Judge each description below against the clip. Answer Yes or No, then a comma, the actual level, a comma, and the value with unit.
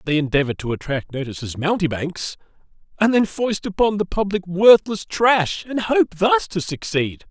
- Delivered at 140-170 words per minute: Yes, average, 165 wpm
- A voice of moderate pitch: Yes, medium, 175 Hz